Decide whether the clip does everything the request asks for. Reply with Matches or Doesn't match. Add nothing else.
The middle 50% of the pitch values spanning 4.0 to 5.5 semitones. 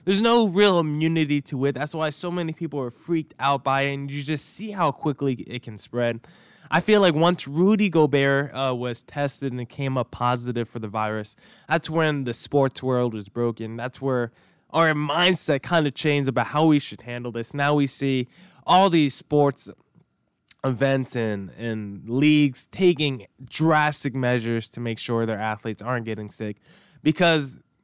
Matches